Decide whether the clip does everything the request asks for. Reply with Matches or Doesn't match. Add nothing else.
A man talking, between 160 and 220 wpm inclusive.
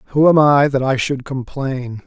Matches